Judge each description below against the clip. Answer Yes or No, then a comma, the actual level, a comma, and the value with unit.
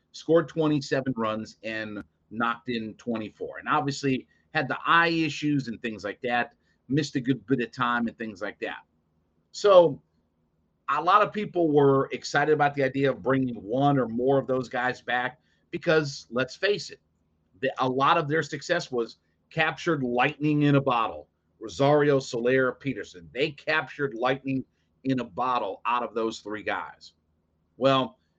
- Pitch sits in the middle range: No, low, 130 Hz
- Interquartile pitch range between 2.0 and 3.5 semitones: No, average, 4.4 semitones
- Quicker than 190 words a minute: No, average, 165 wpm